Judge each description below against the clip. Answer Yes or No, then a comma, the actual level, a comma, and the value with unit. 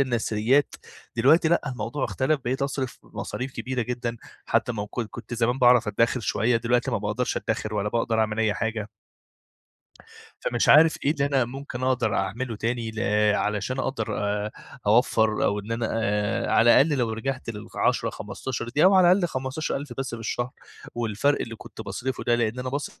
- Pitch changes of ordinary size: Yes, average, 3.1 semitones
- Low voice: Yes, low, 120 Hz